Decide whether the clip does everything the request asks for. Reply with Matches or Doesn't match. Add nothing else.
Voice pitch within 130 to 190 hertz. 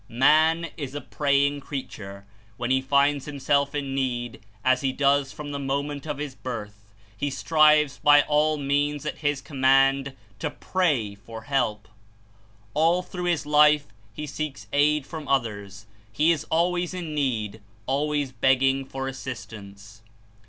Matches